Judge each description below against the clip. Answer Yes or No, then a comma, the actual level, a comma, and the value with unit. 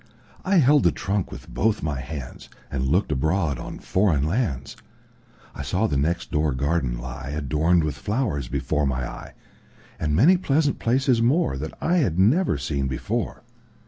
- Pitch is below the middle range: Yes, very low, 80 Hz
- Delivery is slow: No, average, 145 wpm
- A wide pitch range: Yes, wide, 8.3 semitones